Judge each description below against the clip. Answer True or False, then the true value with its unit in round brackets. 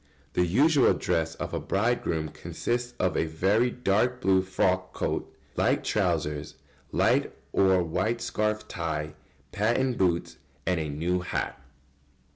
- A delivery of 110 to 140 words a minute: True (135 wpm)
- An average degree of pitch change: False (6.1 semitones)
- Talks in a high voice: False (95 Hz)